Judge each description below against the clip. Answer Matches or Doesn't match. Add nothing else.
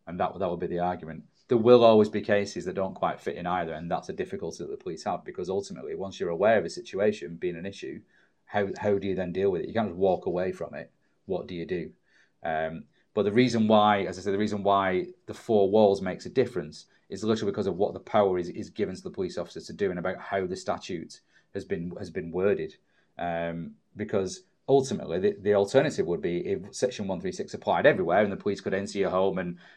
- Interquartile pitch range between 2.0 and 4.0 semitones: Doesn't match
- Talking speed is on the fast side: Matches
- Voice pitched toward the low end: Matches